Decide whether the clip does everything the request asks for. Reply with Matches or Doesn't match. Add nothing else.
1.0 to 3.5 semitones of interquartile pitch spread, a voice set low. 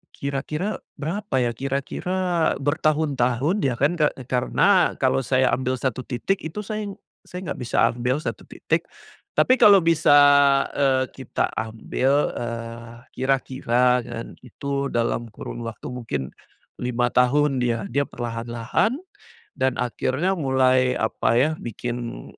Doesn't match